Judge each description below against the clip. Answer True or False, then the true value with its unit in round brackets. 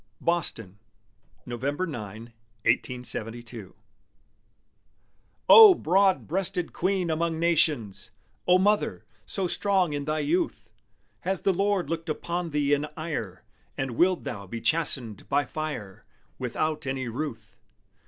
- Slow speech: True (115 wpm)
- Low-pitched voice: False (155 Hz)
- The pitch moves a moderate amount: False (6.7 semitones)